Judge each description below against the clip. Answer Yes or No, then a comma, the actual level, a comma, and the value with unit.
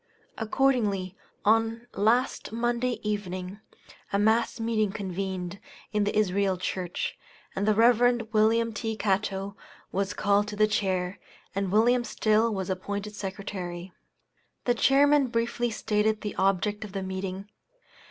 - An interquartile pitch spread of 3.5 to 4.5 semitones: No, average, 2.8 semitones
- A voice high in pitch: Yes, high, 210 Hz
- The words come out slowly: Yes, slow, 130 wpm